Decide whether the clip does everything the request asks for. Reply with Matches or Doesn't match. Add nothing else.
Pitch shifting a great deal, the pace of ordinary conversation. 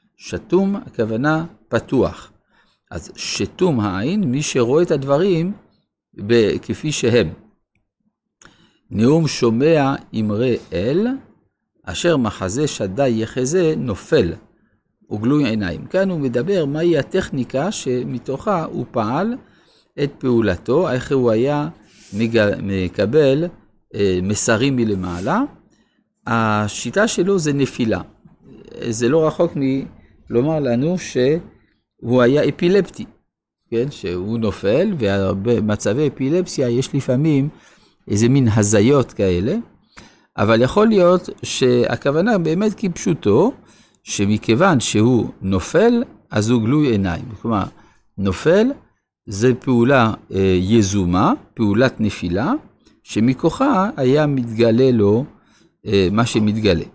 Doesn't match